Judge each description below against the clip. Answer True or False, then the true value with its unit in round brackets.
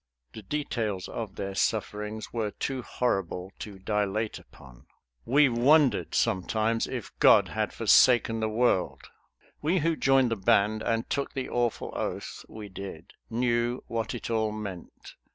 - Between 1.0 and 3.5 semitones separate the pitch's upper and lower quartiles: True (3.2 semitones)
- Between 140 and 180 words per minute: True (145 wpm)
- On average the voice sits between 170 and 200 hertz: False (110 Hz)